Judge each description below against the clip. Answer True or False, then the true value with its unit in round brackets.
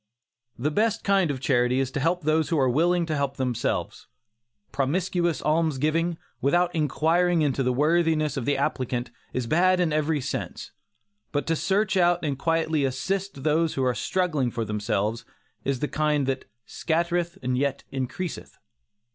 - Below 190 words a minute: True (160 wpm)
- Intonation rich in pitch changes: False (4.4 semitones)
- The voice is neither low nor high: True (150 Hz)